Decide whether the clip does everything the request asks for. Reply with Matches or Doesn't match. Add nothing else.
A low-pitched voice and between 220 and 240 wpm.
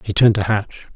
Doesn't match